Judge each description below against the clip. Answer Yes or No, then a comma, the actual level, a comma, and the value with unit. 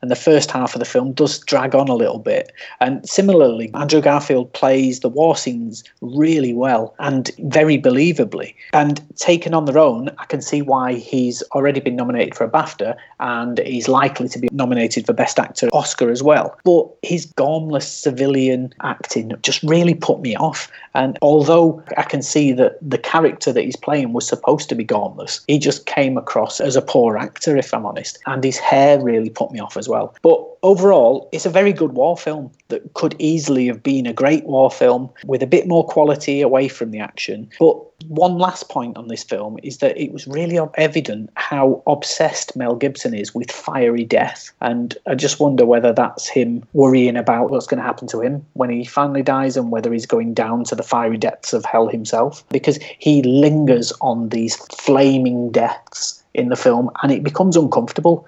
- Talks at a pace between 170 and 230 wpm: Yes, average, 195 wpm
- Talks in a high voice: No, medium, 140 Hz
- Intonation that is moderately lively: Yes, average, 3.9 semitones